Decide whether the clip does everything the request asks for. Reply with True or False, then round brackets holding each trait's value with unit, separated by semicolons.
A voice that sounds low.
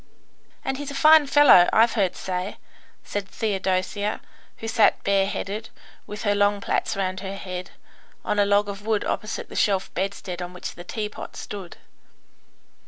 False (205 Hz)